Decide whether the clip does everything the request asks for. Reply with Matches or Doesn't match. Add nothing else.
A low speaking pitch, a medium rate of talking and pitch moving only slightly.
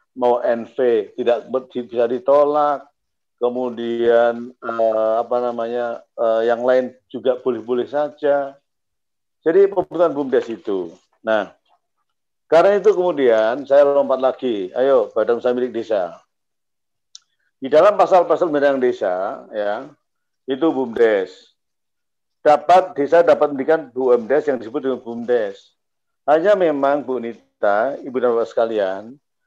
Doesn't match